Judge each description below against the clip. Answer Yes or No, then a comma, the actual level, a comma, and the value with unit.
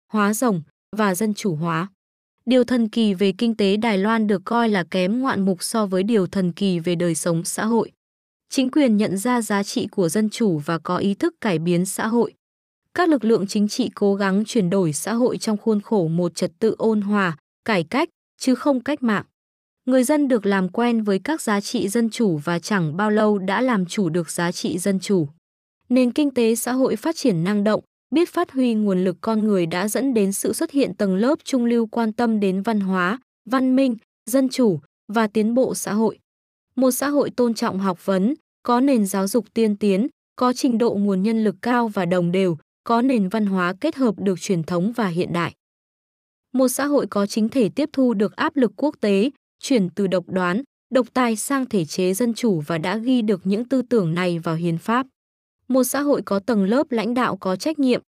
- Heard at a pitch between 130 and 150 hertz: No, high, 220 Hz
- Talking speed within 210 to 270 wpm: Yes, average, 225 wpm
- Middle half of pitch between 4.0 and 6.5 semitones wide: Yes, average, 4.3 semitones